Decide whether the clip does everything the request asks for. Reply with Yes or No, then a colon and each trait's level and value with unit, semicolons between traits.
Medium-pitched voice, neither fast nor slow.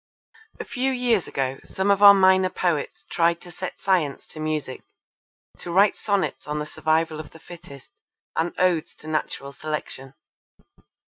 Yes: medium, 165 Hz; average, 155 wpm